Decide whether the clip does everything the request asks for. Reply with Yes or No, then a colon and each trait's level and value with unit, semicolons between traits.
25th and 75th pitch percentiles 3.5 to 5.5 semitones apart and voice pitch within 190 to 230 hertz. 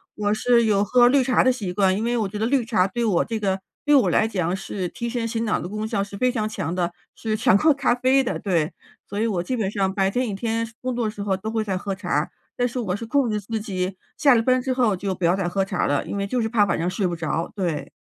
Yes: average, 3.8 semitones; high, 210 Hz